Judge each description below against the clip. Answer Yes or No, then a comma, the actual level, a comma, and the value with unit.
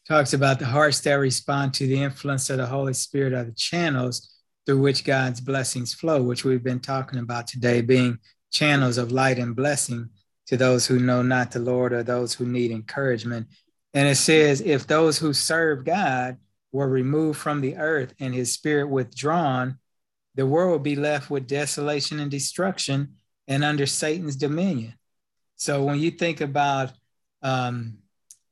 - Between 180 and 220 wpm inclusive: No, average, 170 wpm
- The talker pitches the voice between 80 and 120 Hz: No, low, 135 Hz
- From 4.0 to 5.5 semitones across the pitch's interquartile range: No, average, 2.8 semitones